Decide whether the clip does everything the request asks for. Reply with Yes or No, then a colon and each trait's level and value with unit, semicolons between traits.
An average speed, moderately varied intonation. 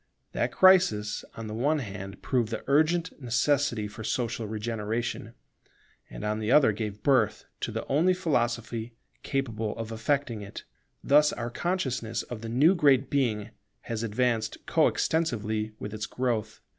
Yes: average, 150 wpm; average, 4.3 semitones